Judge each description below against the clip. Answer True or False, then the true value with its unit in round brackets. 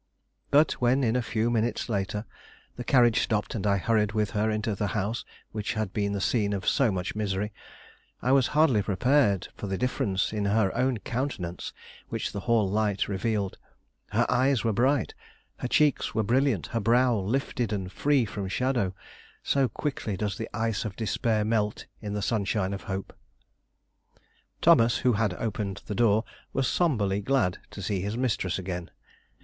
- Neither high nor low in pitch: False (110 Hz)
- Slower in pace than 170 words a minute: False (175 wpm)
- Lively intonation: False (3.2 semitones)